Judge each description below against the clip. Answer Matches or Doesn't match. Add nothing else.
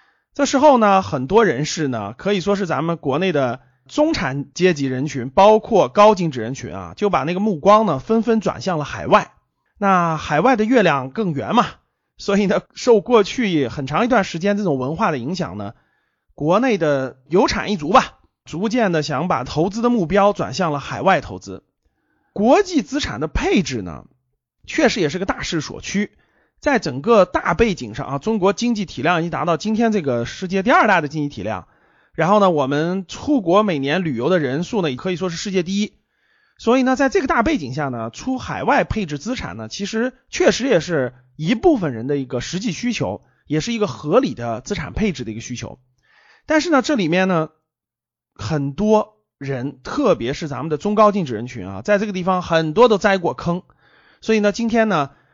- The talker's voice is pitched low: Doesn't match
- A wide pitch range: Matches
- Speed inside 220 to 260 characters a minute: Doesn't match